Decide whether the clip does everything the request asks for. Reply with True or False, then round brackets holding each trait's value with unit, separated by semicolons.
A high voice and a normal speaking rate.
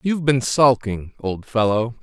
False (120 Hz; 150 wpm)